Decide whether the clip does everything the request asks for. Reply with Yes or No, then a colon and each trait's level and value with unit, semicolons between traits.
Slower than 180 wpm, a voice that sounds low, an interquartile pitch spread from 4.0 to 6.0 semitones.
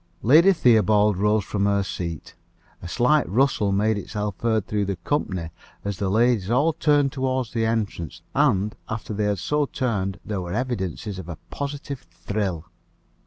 Yes: average, 165 wpm; low, 105 Hz; average, 4.5 semitones